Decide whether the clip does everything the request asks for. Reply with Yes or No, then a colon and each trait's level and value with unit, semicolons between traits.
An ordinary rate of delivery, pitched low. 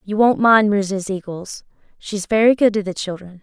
No: average, 195 wpm; high, 200 Hz